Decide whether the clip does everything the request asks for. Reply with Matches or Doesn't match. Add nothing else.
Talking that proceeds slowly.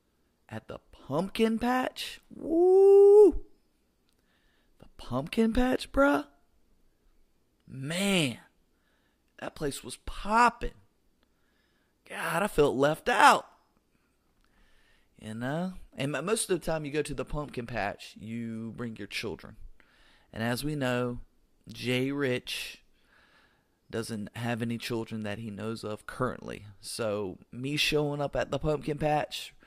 Matches